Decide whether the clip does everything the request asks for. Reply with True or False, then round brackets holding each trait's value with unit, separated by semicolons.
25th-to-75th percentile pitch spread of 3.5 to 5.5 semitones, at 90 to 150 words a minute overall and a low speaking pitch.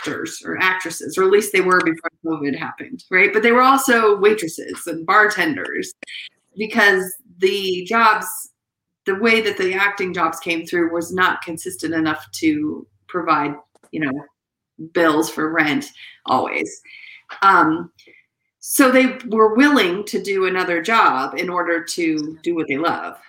False (4.9 semitones; 145 wpm; 185 Hz)